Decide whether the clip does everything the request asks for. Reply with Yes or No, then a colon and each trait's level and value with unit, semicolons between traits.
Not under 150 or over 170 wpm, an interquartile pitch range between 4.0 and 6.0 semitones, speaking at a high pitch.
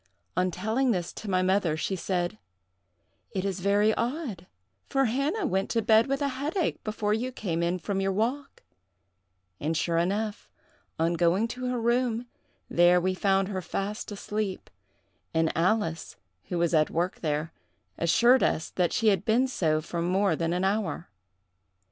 Yes: average, 165 wpm; average, 4.6 semitones; high, 195 Hz